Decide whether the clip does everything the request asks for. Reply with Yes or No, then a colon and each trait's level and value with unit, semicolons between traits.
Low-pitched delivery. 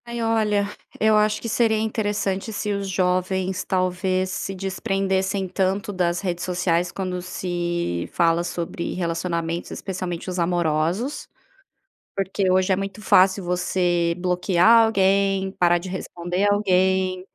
No: medium, 185 Hz